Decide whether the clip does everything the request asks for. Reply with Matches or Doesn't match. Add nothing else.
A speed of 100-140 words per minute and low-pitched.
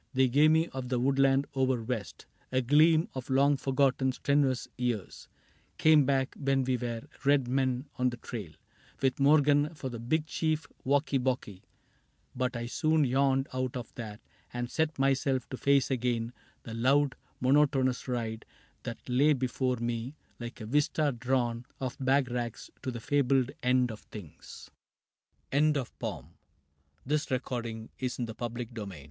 Matches